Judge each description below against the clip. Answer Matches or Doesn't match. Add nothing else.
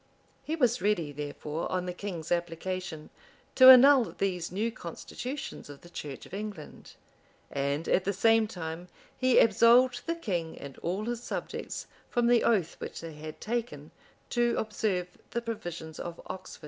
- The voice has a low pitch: Doesn't match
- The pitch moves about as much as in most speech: Doesn't match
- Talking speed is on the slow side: Doesn't match